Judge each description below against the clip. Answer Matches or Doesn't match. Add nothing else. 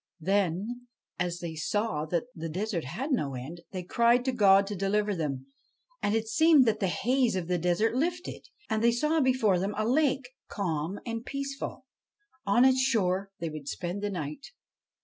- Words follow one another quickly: Doesn't match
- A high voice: Matches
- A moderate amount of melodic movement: Doesn't match